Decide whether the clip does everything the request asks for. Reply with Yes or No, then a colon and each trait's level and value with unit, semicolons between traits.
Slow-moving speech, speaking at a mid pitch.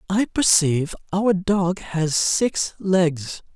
Yes: slow, 120 wpm; medium, 180 Hz